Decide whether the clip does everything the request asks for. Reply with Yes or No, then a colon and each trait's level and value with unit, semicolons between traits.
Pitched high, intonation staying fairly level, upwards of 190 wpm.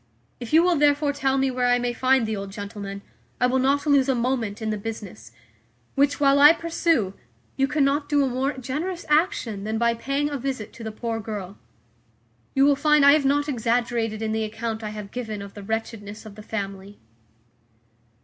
No: high, 245 Hz; average, 4.5 semitones; average, 200 wpm